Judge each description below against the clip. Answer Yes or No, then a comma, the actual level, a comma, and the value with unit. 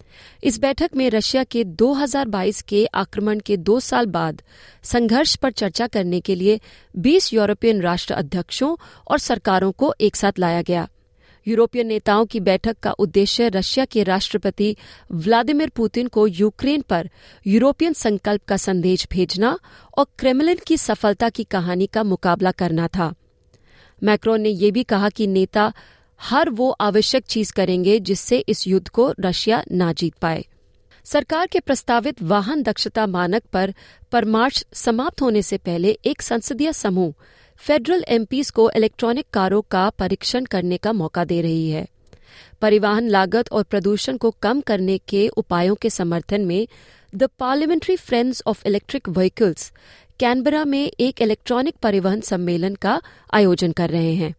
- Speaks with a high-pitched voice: Yes, high, 215 Hz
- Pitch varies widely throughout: No, average, 4.5 semitones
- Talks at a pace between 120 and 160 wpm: Yes, average, 150 wpm